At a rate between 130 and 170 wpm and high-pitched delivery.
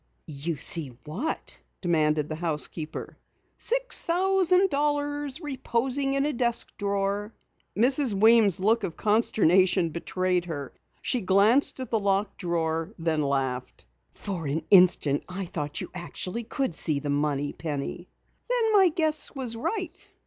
Yes: average, 140 wpm; high, 195 Hz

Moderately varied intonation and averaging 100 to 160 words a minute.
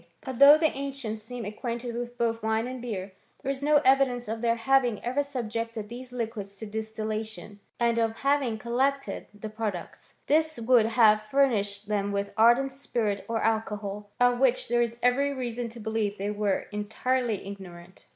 No: average, 3.0 semitones; average, 180 wpm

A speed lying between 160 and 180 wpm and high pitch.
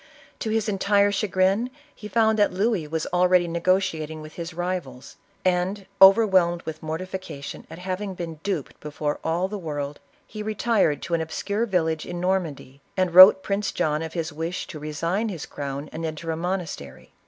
No: average, 170 wpm; medium, 175 Hz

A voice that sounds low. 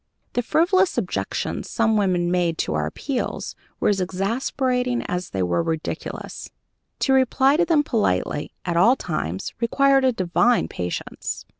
No: high, 225 Hz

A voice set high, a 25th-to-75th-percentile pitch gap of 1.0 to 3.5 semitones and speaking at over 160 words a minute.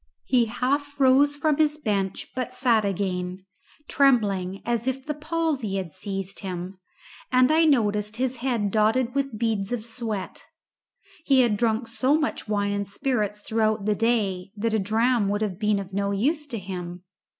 No: high, 220 Hz; average, 4.5 semitones; average, 170 wpm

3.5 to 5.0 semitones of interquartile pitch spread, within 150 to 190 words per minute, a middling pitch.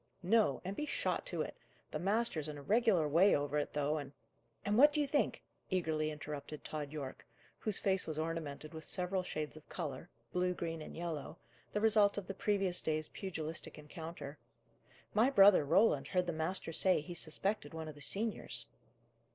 Yes: average, 4.4 semitones; average, 185 wpm; medium, 165 Hz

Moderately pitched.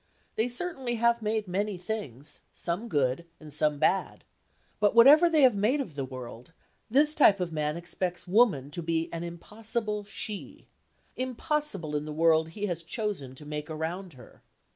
Yes: medium, 180 Hz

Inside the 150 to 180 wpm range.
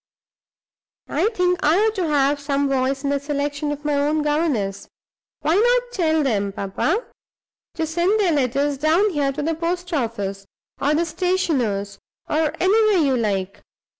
Yes: average, 160 wpm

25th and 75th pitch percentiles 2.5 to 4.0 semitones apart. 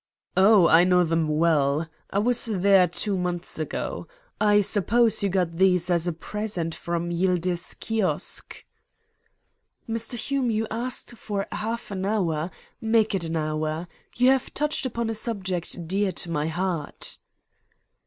No: average, 4.5 semitones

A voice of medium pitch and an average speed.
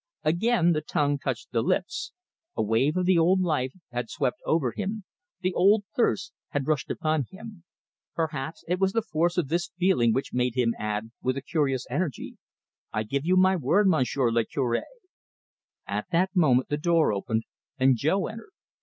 Yes: medium, 155 Hz; average, 180 wpm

